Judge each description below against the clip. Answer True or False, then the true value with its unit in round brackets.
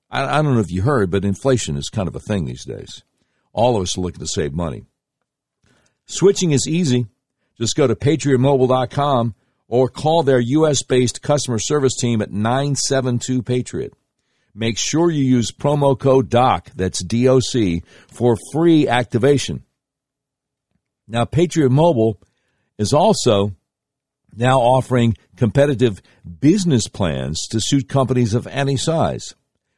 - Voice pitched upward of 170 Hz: False (130 Hz)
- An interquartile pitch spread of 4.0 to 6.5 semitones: False (3.4 semitones)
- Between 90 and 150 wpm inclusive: True (135 wpm)